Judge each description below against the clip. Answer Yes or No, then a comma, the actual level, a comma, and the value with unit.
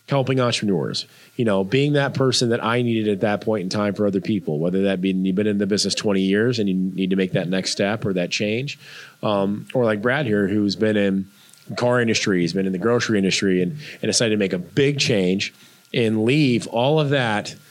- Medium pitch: No, low, 105 Hz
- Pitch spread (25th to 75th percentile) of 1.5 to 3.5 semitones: No, average, 3.9 semitones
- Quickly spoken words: Yes, fast, 230 wpm